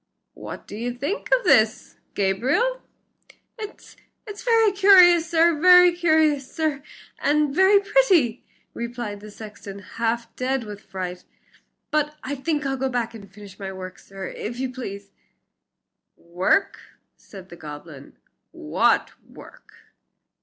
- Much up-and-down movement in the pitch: Yes, wide, 9.0 semitones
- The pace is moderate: No, slow, 130 wpm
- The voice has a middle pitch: No, very high, 255 Hz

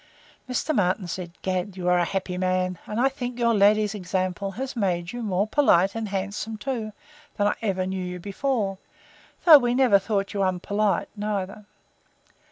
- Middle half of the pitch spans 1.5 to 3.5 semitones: Yes, average, 3.2 semitones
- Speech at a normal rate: Yes, average, 175 wpm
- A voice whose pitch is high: Yes, high, 200 Hz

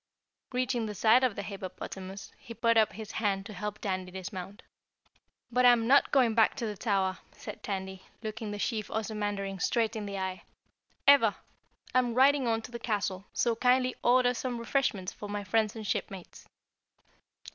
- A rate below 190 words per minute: Yes, average, 170 wpm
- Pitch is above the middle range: Yes, high, 215 Hz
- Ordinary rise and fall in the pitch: Yes, average, 3.4 semitones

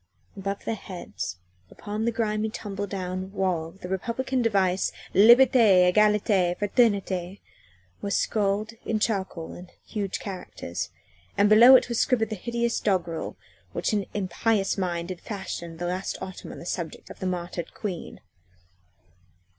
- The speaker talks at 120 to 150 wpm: Yes, average, 140 wpm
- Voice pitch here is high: Yes, high, 195 Hz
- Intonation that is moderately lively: Yes, average, 3.1 semitones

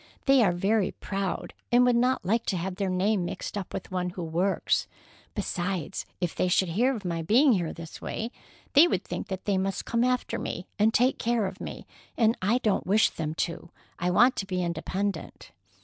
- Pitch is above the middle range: Yes, high, 195 Hz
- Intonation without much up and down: No, average, 4.3 semitones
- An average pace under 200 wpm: No, fast, 205 wpm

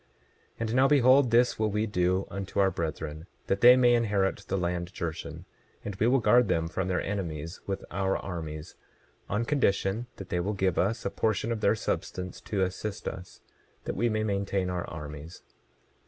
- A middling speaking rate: Yes, average, 185 wpm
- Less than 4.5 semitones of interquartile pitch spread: Yes, average, 3.7 semitones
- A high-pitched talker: No, low, 100 Hz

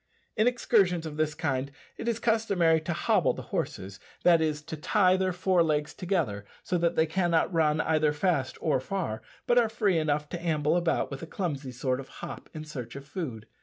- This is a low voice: No, medium, 160 Hz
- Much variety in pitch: No, average, 3.7 semitones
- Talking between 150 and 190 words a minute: No, fast, 205 wpm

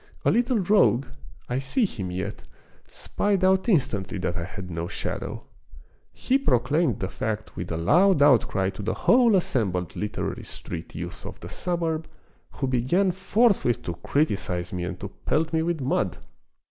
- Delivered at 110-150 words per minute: No, average, 160 wpm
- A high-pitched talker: No, low, 130 Hz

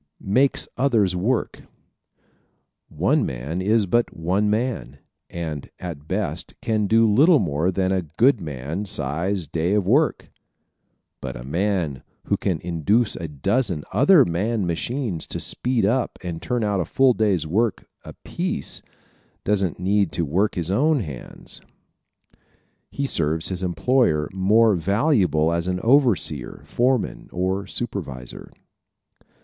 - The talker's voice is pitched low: Yes, very low, 95 Hz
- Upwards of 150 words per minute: No, slow, 135 wpm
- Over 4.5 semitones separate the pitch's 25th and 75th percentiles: Yes, wide, 5.5 semitones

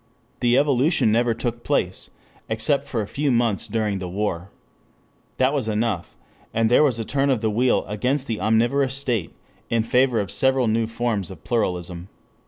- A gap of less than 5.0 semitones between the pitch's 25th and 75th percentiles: Yes, average, 3.4 semitones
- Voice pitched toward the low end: Yes, low, 115 Hz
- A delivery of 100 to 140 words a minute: No, average, 175 wpm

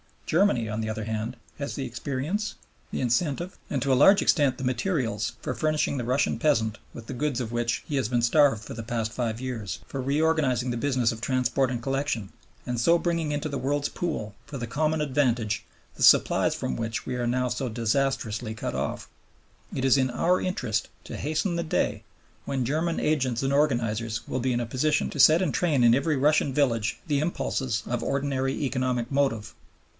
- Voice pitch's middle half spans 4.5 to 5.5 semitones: No, average, 3.8 semitones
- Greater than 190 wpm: Yes, average, 200 wpm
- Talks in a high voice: No, low, 130 Hz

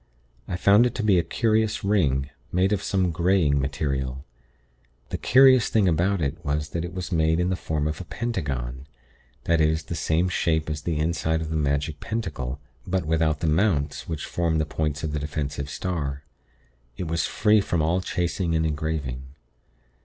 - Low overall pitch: Yes, very low, 80 Hz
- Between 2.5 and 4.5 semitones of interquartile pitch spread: Yes, average, 3.8 semitones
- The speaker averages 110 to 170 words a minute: No, average, 185 wpm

